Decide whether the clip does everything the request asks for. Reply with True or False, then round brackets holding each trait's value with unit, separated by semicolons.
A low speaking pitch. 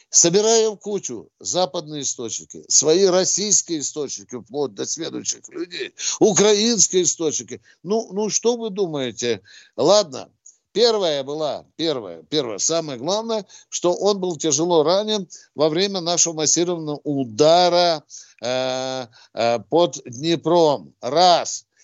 False (170 Hz)